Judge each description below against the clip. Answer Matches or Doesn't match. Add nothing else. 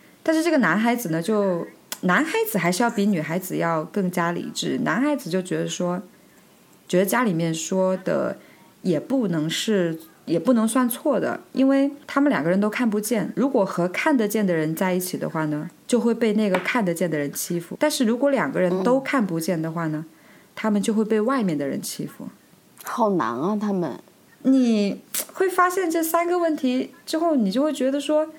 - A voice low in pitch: Doesn't match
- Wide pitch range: Matches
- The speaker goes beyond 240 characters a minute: Matches